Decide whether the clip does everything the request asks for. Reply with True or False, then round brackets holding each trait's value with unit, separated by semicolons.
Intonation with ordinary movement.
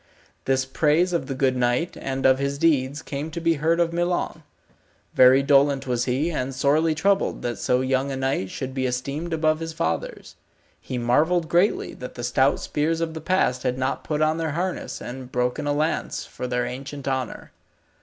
True (3.8 semitones)